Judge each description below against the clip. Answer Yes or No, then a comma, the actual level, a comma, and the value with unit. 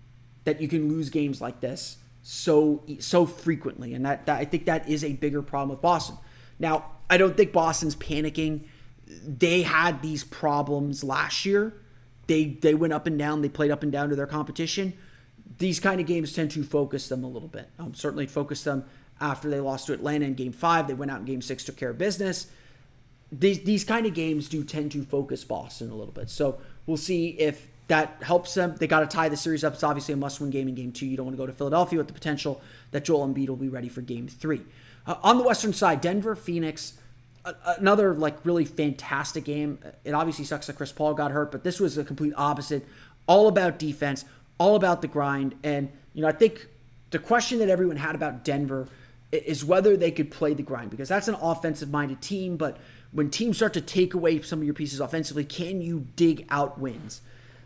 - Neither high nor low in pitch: Yes, medium, 150 Hz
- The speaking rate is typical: No, fast, 220 wpm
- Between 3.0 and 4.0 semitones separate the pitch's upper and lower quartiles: Yes, average, 3.3 semitones